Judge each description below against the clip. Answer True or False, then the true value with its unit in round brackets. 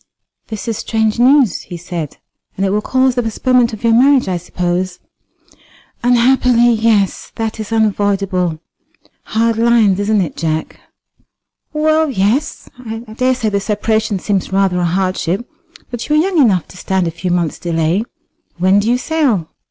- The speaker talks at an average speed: True (160 wpm)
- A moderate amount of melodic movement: True (4.4 semitones)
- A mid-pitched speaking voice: False (215 Hz)